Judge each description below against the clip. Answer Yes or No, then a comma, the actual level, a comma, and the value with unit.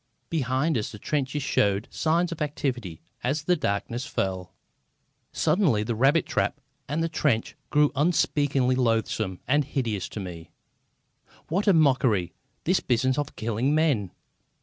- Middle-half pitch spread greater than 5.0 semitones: Yes, wide, 5.5 semitones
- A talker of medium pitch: No, low, 130 Hz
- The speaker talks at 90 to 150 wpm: Yes, average, 140 wpm